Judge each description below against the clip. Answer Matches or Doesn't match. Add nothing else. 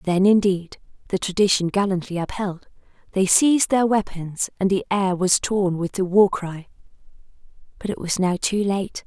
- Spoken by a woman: Matches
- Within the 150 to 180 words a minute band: Matches